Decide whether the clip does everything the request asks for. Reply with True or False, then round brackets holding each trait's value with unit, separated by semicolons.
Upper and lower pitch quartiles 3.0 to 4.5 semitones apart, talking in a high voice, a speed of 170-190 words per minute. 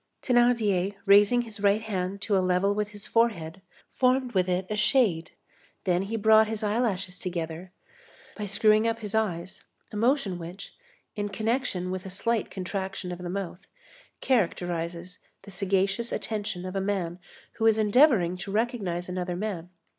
False (3.3 semitones; 200 Hz; 160 wpm)